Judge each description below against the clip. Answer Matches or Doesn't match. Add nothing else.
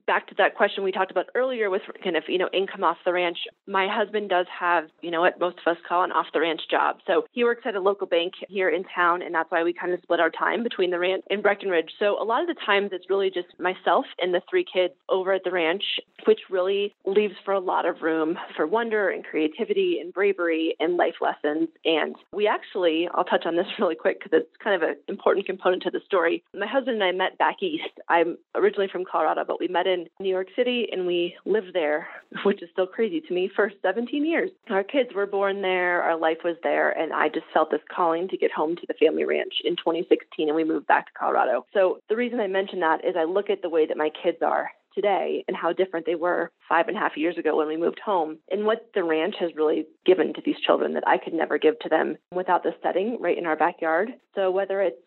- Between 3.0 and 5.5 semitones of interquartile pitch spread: Matches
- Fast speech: Matches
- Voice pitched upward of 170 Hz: Matches